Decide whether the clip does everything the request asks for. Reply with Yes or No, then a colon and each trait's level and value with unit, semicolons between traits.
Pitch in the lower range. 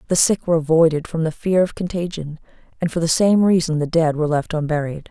No: medium, 165 Hz